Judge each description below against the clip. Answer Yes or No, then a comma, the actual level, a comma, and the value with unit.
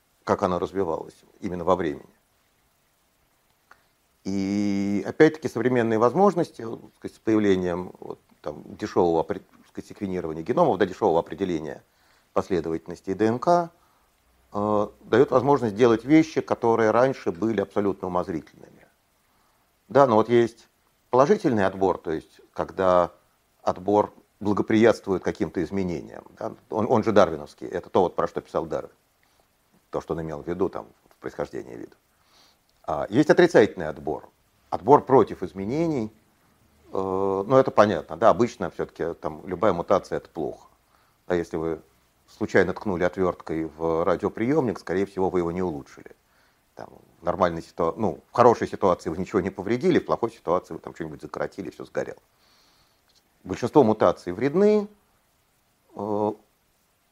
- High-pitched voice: No, low, 105 Hz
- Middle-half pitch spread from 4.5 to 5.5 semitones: Yes, average, 4.8 semitones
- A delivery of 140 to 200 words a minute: No, average, 130 wpm